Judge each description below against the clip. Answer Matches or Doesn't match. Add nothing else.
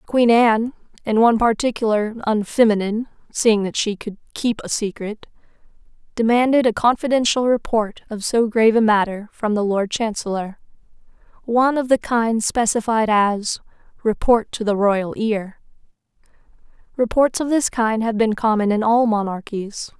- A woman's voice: Matches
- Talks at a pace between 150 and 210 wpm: Doesn't match